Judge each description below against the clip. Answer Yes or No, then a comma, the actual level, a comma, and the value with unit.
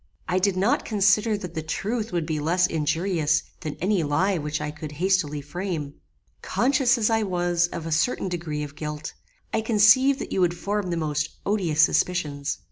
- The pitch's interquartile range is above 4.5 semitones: Yes, average, 4.9 semitones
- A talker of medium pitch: Yes, medium, 175 Hz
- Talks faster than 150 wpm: Yes, average, 185 wpm